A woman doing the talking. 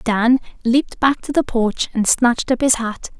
Yes: female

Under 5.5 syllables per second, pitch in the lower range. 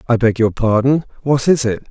Yes: 5.2 syllables/s; low, 125 Hz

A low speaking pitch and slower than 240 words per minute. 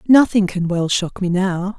No: high, 190 Hz; average, 200 wpm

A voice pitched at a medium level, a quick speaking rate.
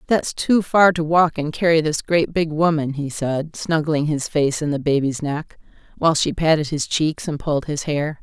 Yes: medium, 155 Hz; fast, 210 wpm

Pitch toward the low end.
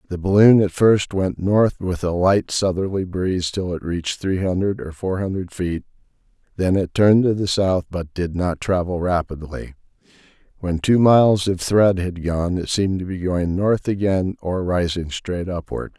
Yes: very low, 90 Hz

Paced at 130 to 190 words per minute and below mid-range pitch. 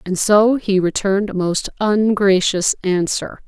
No: average, 140 wpm; high, 200 Hz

